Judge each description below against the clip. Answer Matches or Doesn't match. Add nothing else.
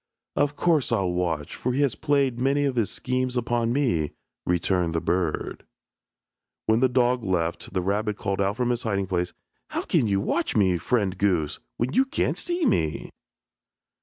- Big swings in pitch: Matches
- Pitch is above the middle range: Doesn't match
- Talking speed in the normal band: Matches